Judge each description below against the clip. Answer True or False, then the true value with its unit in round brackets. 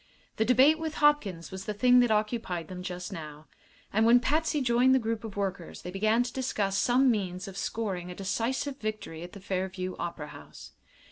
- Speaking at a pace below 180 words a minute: False (195 wpm)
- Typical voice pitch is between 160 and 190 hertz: False (215 Hz)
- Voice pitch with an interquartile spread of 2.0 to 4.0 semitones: False (5.0 semitones)